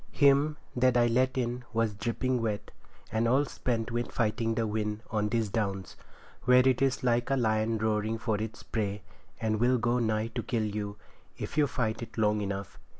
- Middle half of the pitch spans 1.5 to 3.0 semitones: Yes, narrow, 2.4 semitones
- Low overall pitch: Yes, low, 115 Hz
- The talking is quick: No, average, 190 wpm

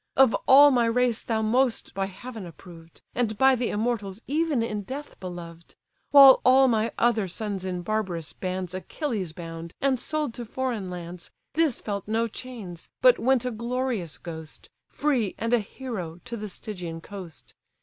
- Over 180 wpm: No, average, 165 wpm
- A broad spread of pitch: Yes, wide, 5.7 semitones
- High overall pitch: Yes, high, 220 Hz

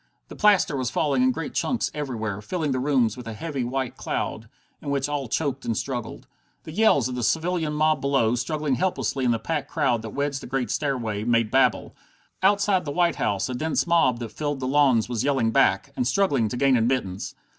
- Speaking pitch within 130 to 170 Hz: Yes, low, 135 Hz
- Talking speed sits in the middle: No, fast, 210 wpm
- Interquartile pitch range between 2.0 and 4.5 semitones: Yes, average, 4.0 semitones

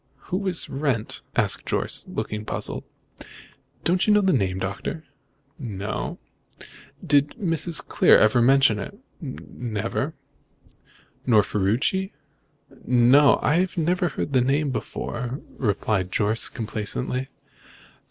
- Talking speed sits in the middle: No, slow, 110 wpm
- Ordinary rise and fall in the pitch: No, wide, 6.8 semitones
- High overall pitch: No, low, 130 Hz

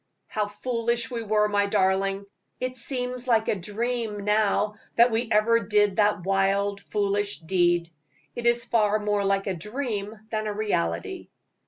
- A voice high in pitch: Yes, high, 210 Hz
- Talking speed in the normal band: Yes, average, 155 wpm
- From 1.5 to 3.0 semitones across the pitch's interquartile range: Yes, narrow, 2.6 semitones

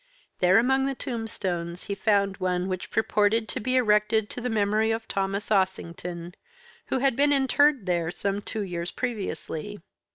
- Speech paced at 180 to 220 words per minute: No, average, 160 wpm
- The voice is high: Yes, high, 210 Hz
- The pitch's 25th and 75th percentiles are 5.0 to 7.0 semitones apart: No, average, 3.8 semitones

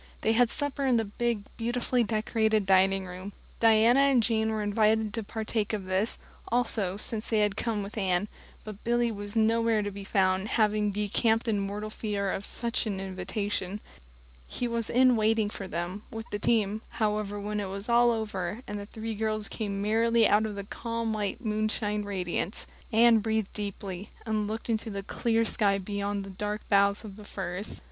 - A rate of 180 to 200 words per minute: Yes, average, 185 wpm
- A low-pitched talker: No, high, 215 Hz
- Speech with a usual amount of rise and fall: No, narrow, 2.0 semitones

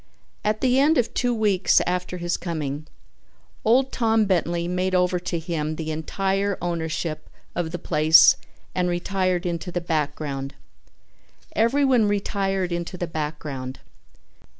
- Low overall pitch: No, medium, 180 Hz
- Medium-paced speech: No, slow, 130 wpm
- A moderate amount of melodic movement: Yes, average, 3.7 semitones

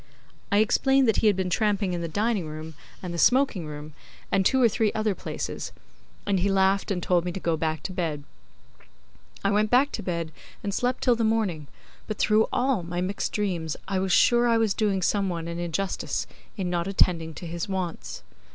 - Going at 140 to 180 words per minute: No, fast, 205 wpm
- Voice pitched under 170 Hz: No, high, 190 Hz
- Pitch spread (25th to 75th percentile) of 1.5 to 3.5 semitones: No, average, 3.9 semitones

